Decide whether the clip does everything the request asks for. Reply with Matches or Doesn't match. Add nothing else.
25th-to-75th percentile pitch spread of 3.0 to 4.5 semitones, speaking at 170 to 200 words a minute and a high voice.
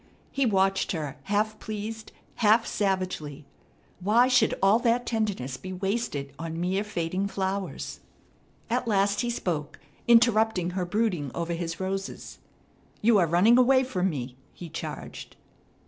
Doesn't match